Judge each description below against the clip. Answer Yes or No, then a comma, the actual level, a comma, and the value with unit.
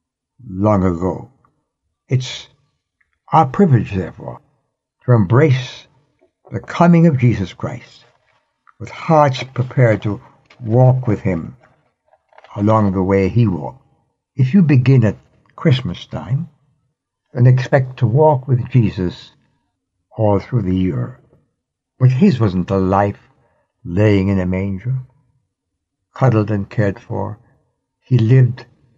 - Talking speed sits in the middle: No, slow, 115 wpm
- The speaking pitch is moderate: No, low, 120 Hz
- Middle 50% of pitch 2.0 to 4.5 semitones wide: No, average, 5.1 semitones